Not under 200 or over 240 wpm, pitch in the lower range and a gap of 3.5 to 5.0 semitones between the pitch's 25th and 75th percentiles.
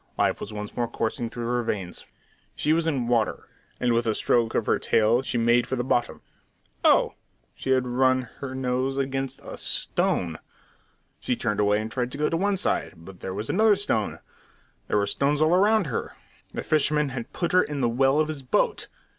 Yes: fast, 205 wpm; low, 125 Hz; average, 4.0 semitones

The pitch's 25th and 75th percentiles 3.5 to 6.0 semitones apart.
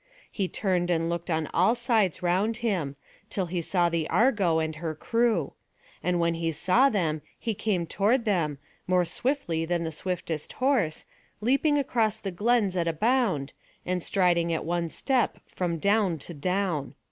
Yes: average, 4.8 semitones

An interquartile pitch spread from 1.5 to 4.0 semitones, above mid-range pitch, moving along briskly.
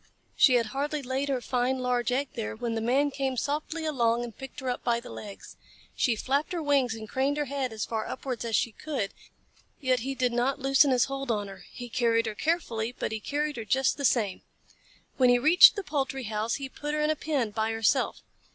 Yes: average, 3.5 semitones; very high, 255 Hz; fast, 225 wpm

